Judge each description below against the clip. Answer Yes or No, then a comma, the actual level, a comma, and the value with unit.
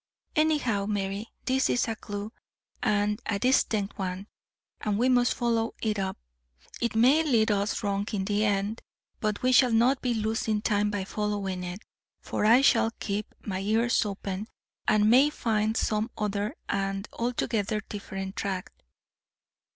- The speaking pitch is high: Yes, high, 210 Hz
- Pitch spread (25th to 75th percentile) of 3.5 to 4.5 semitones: No, narrow, 2.5 semitones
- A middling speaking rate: Yes, average, 150 wpm